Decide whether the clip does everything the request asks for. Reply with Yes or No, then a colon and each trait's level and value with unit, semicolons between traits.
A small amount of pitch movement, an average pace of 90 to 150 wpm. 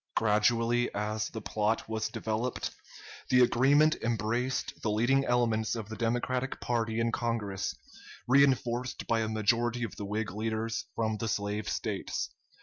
Yes: narrow, 2.0 semitones; average, 145 wpm